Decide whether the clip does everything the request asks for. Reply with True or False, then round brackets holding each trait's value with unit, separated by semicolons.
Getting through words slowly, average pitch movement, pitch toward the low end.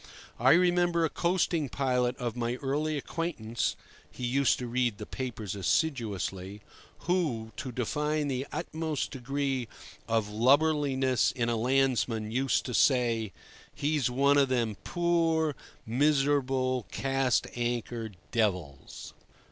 True (120 wpm; 3.8 semitones; 130 Hz)